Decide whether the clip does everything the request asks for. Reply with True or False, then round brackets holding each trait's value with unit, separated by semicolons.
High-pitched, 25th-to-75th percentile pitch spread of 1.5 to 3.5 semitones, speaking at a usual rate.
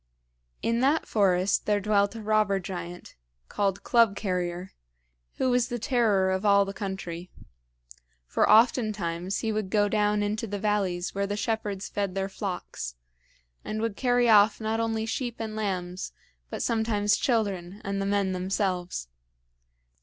True (205 Hz; 2.5 semitones; 150 wpm)